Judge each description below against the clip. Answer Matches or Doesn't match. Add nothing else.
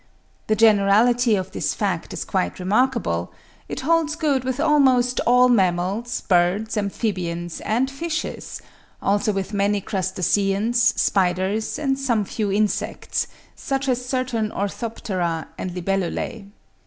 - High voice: Matches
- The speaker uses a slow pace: Matches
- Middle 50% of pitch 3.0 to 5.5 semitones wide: Matches